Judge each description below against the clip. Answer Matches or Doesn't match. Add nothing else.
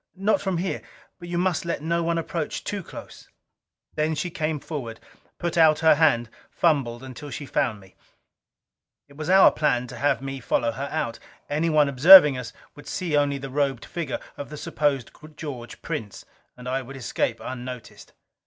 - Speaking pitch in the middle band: Matches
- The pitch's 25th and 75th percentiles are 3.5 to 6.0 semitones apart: Matches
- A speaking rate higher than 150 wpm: Matches